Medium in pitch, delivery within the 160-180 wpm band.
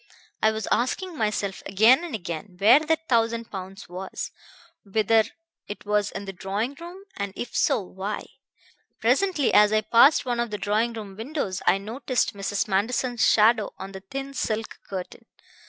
No: high, 220 Hz; average, 165 wpm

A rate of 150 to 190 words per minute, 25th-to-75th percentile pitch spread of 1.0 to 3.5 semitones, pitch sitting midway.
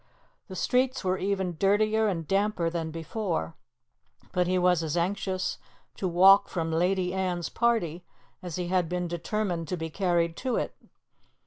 Yes: average, 155 wpm; narrow, 2.6 semitones; medium, 180 Hz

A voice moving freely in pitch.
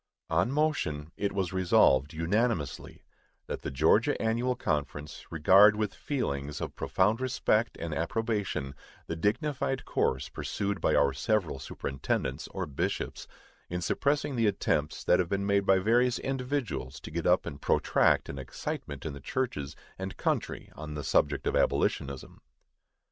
Yes: wide, 7.6 semitones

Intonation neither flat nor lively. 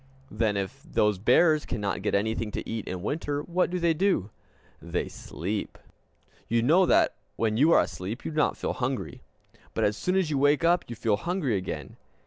No: wide, 7.5 semitones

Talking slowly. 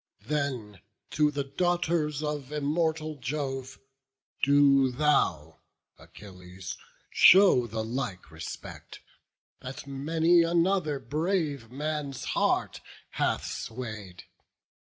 Yes: slow, 90 wpm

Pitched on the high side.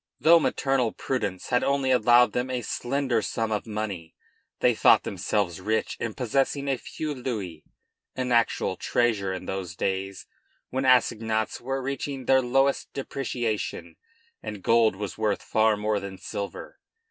No: low, 115 Hz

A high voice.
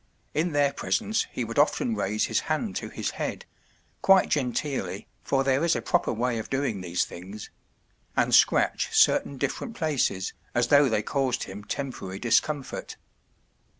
No: low, 135 Hz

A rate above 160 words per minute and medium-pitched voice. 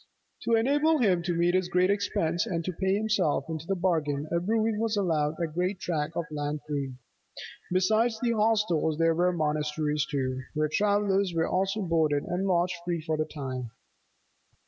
Yes: average, 180 wpm; medium, 175 Hz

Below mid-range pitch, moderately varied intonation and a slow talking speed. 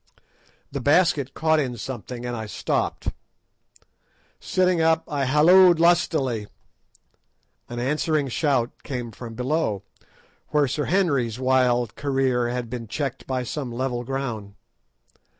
Yes: low, 130 Hz; average, 3.9 semitones; slow, 120 wpm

